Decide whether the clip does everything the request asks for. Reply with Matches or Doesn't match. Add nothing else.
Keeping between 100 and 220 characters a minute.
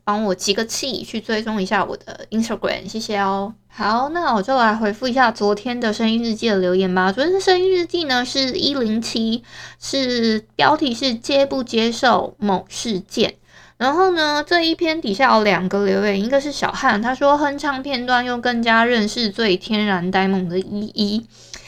Doesn't match